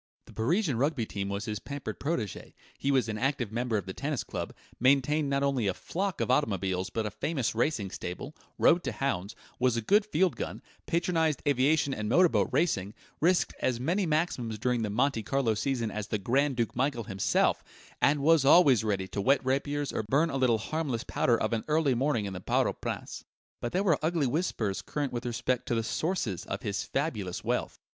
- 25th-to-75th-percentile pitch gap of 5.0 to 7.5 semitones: Yes, average, 5.3 semitones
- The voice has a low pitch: Yes, low, 130 Hz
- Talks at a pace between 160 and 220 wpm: Yes, fast, 205 wpm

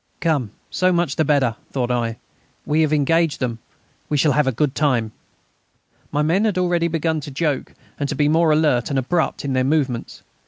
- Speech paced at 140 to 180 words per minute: No, average, 195 wpm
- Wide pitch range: No, average, 3.6 semitones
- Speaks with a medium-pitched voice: Yes, medium, 150 Hz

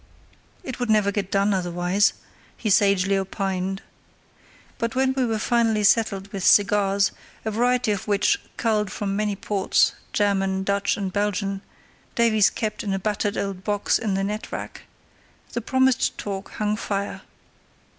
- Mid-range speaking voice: No, high, 205 Hz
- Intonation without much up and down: Yes, narrow, 1.9 semitones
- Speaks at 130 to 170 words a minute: Yes, average, 145 wpm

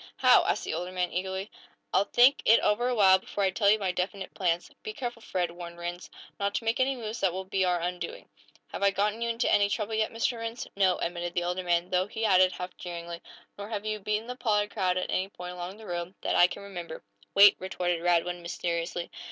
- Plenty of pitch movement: No, average, 3.2 semitones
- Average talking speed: No, fast, 235 wpm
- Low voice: No, high, 190 Hz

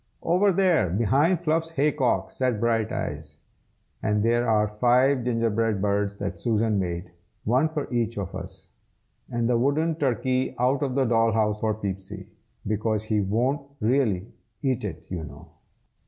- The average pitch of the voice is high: No, low, 115 Hz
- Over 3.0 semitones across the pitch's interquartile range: Yes, average, 4.1 semitones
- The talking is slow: No, average, 155 wpm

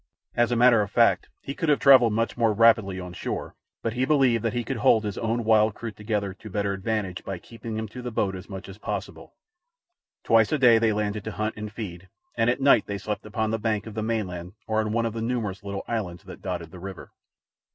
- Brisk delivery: Yes, fast, 240 wpm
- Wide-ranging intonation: No, narrow, 2.6 semitones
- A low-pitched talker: Yes, low, 110 Hz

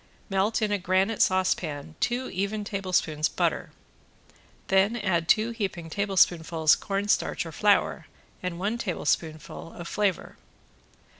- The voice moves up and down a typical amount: Yes, average, 3.3 semitones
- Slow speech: Yes, slow, 120 wpm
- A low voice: No, high, 190 Hz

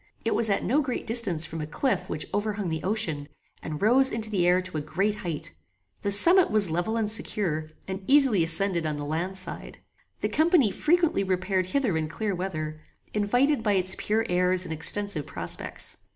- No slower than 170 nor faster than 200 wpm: Yes, average, 190 wpm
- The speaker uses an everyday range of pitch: Yes, average, 4.9 semitones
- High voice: Yes, high, 195 Hz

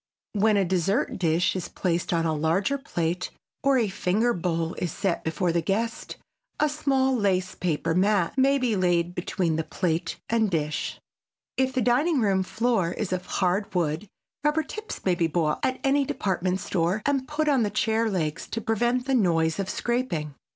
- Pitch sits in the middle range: No, high, 195 Hz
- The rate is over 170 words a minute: Yes, average, 180 wpm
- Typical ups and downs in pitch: No, wide, 6.0 semitones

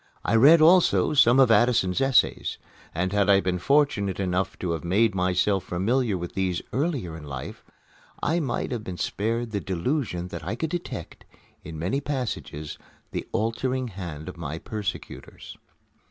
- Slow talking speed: No, average, 160 wpm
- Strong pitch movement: Yes, wide, 6.1 semitones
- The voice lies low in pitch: Yes, low, 100 Hz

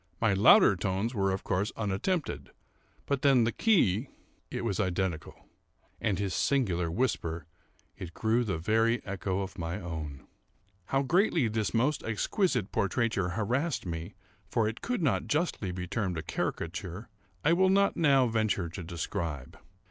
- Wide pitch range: Yes, wide, 5.8 semitones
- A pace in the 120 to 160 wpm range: Yes, average, 150 wpm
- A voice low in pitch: Yes, low, 105 Hz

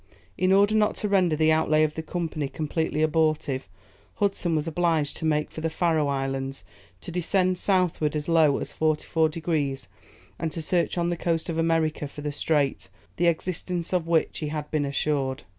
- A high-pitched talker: No, medium, 160 Hz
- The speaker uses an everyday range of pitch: No, narrow, 2.3 semitones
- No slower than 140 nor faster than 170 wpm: No, average, 190 wpm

